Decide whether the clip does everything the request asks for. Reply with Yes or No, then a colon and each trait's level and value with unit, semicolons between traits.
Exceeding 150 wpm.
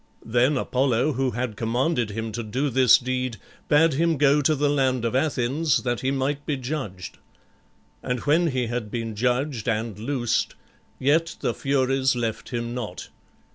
Yes: average, 165 wpm